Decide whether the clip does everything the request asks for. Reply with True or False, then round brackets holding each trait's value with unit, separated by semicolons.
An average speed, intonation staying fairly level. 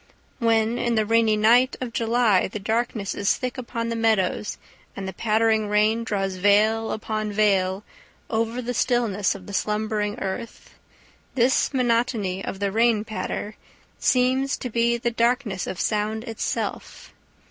True (145 wpm; 2.1 semitones)